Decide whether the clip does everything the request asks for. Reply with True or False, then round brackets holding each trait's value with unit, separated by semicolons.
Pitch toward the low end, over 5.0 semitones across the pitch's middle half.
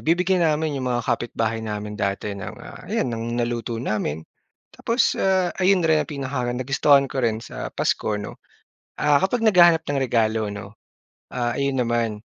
True (125 Hz; 5.5 semitones)